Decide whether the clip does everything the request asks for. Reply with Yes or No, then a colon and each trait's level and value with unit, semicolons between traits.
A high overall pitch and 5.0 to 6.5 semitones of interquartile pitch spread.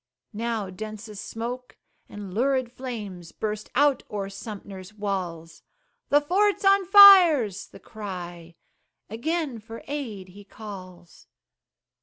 Yes: high, 215 Hz; average, 5.3 semitones